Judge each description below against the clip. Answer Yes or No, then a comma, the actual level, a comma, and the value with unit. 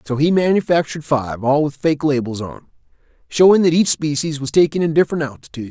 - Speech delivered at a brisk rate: No, average, 190 wpm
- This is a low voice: No, medium, 150 Hz